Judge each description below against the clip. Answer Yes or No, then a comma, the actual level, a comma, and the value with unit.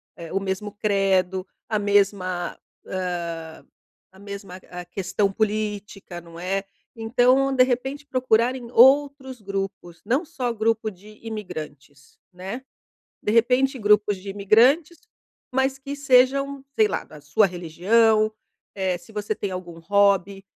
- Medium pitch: No, high, 205 Hz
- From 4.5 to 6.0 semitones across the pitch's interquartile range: Yes, average, 5.0 semitones